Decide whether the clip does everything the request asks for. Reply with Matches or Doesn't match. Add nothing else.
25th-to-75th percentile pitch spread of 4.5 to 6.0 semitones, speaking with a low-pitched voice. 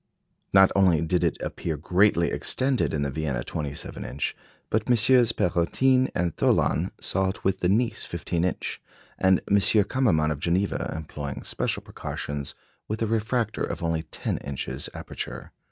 Matches